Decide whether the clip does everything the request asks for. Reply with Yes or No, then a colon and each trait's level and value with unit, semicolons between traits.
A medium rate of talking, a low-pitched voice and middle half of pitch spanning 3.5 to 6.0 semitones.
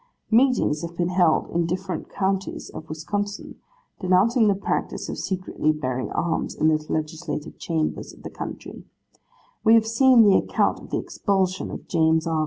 No: average, 165 wpm; medium, 180 Hz; average, 4.2 semitones